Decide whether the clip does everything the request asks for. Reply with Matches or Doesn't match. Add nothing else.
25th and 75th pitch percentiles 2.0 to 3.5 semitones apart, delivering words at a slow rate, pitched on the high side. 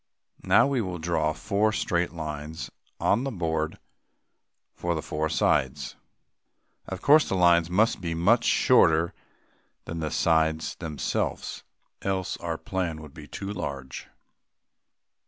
Doesn't match